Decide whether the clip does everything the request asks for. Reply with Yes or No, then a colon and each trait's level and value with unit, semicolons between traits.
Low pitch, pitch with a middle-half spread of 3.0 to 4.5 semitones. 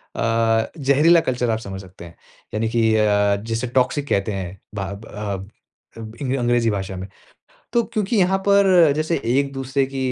No: low, 120 Hz; wide, 5.6 semitones